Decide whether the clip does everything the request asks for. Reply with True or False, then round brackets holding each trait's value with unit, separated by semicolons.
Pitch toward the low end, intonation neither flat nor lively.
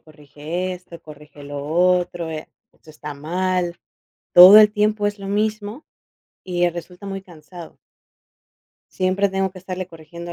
False (180 Hz; 3.2 semitones)